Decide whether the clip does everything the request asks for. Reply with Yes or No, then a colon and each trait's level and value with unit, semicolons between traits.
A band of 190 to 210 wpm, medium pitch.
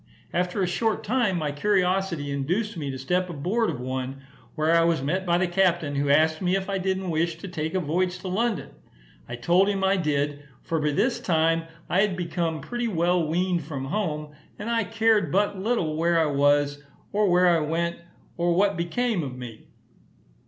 Yes: average, 195 wpm; medium, 170 Hz